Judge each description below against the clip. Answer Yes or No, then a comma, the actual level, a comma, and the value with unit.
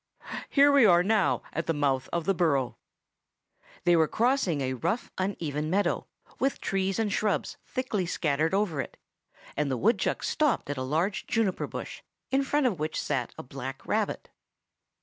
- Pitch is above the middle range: No, medium, 175 Hz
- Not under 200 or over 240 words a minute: No, average, 170 wpm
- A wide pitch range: Yes, wide, 6.6 semitones